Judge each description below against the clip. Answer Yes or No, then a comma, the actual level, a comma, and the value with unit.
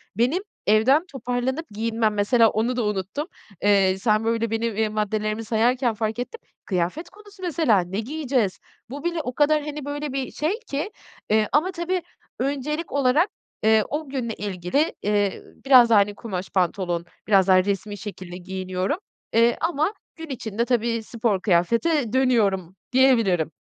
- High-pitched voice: Yes, high, 230 Hz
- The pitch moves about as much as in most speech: No, wide, 5.7 semitones